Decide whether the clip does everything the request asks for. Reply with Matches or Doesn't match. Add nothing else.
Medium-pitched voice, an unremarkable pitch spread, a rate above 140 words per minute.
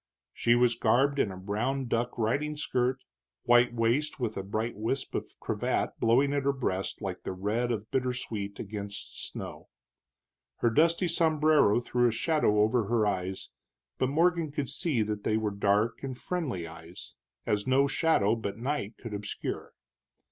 Doesn't match